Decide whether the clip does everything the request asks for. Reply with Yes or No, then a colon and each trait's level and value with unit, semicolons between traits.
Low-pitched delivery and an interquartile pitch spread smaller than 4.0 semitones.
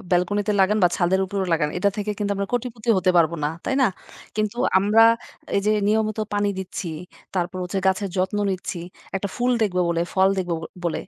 No: high, 195 Hz; average, 2.7 semitones